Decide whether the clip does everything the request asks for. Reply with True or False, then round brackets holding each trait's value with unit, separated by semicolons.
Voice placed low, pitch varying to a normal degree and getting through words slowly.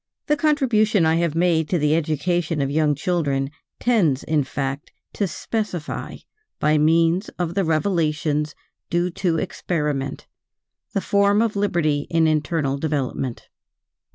False (160 Hz; 3.4 semitones; 130 wpm)